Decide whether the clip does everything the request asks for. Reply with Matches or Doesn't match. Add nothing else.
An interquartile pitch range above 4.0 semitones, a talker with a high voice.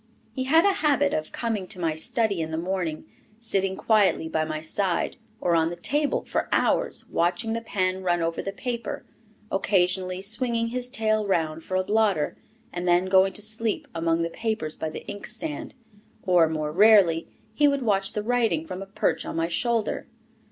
Matches